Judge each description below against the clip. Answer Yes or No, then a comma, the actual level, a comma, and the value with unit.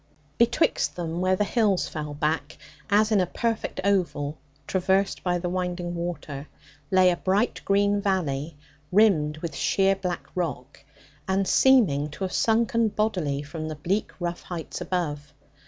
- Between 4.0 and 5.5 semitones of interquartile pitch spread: Yes, average, 4.3 semitones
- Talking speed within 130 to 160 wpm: Yes, average, 150 wpm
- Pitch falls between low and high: Yes, medium, 180 Hz